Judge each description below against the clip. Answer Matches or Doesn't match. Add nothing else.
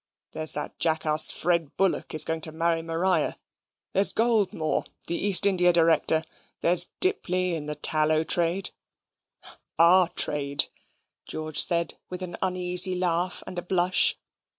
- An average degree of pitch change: Doesn't match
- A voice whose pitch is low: Doesn't match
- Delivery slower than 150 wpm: Matches